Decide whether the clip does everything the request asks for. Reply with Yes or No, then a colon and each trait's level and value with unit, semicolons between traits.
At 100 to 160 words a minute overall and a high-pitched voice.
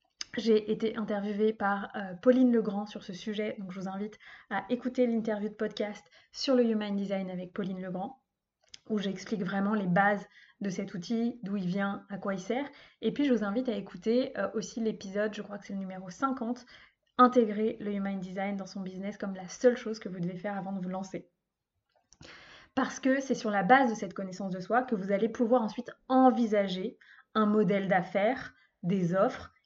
No: average, 200 wpm; high, 210 Hz